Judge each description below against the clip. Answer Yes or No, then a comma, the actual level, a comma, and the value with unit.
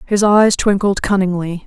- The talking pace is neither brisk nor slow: Yes, average, 145 wpm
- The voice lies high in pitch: Yes, high, 195 Hz